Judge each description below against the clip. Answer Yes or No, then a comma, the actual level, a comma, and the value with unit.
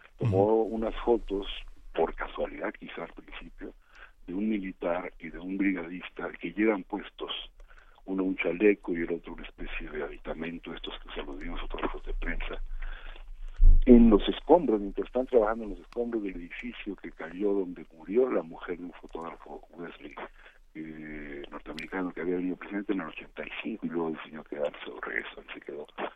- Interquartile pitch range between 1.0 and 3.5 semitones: No, average, 3.9 semitones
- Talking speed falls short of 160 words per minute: No, average, 170 wpm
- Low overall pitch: Yes, very low, 95 Hz